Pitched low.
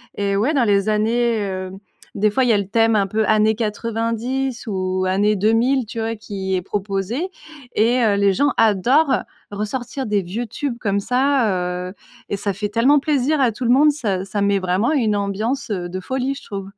No: high, 215 Hz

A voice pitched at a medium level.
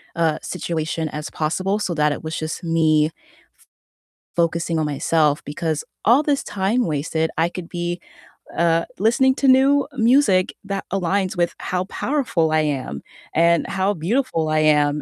Yes: medium, 170 Hz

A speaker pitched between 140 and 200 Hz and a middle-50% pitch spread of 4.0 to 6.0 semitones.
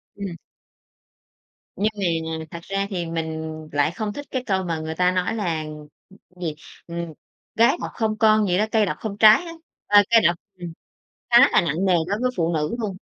Yes: high, 190 Hz; average, 4.3 semitones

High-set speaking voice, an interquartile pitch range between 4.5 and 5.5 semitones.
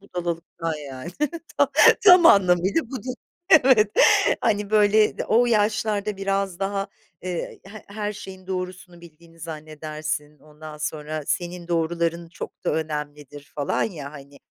No: medium, 175 Hz; average, 4.9 semitones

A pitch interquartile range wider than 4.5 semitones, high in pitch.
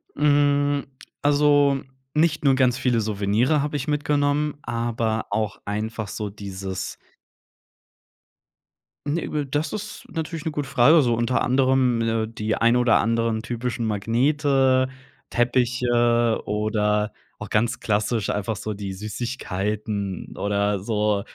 No: average, 4.9 semitones; low, 120 Hz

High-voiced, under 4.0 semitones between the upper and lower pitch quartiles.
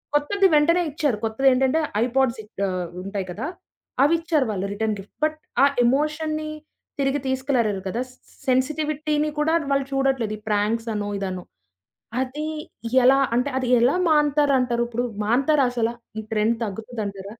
No: very high, 260 Hz; average, 5.1 semitones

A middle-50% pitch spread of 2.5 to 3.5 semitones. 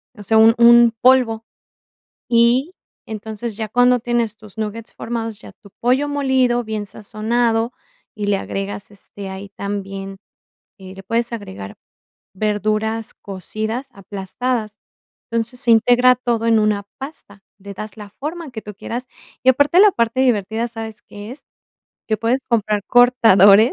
Yes: average, 2.8 semitones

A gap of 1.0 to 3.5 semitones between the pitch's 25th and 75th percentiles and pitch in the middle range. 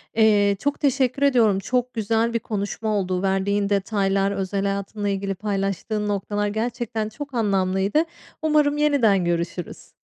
No: average, 3.0 semitones; high, 205 Hz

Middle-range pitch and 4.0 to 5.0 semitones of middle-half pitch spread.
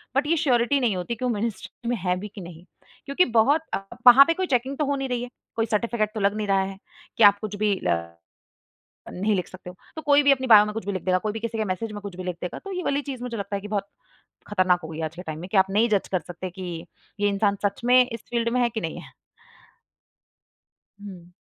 No: high, 210 Hz; average, 4.6 semitones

